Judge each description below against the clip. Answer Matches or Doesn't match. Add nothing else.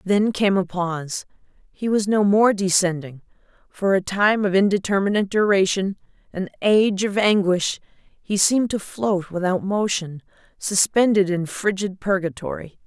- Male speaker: Doesn't match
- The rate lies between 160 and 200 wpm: Doesn't match